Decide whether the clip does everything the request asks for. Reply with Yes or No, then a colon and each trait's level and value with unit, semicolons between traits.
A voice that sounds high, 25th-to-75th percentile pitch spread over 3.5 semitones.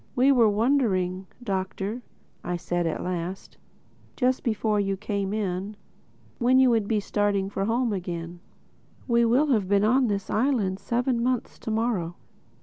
Yes: high, 210 Hz; average, 3.9 semitones